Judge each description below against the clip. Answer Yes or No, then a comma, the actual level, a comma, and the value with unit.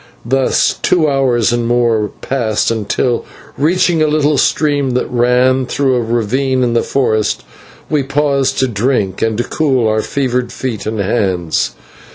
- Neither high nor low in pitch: No, low, 125 Hz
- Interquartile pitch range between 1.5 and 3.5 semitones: Yes, average, 3.1 semitones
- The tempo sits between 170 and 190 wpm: No, average, 155 wpm